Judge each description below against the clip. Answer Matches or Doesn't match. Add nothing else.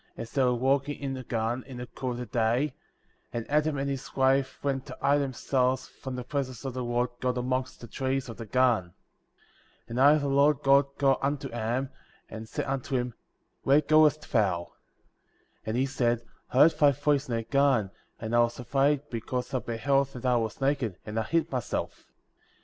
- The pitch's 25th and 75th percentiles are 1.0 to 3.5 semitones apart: Matches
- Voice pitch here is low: Matches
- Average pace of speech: Doesn't match